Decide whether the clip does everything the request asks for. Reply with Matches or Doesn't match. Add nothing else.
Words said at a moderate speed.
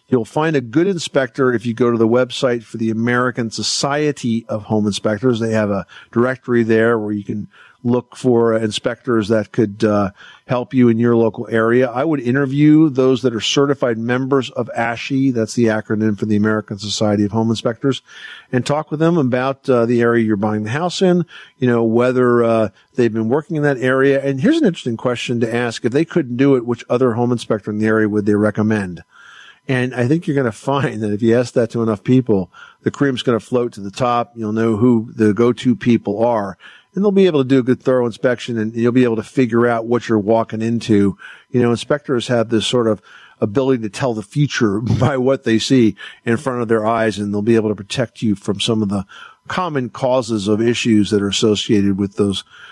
Doesn't match